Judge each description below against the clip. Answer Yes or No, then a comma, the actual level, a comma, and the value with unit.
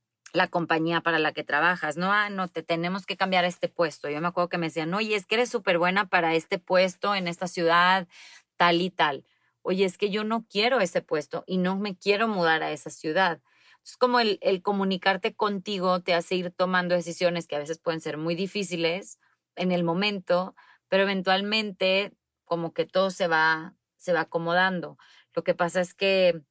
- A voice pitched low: No, medium, 180 Hz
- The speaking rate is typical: No, fast, 200 wpm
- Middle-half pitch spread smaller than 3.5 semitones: Yes, narrow, 2.6 semitones